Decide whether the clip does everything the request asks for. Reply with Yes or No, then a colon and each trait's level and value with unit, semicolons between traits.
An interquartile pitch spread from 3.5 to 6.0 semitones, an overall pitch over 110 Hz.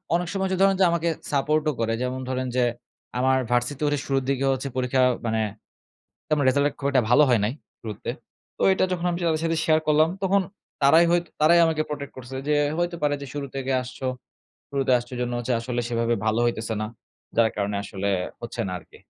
Yes: average, 4.3 semitones; low, 135 Hz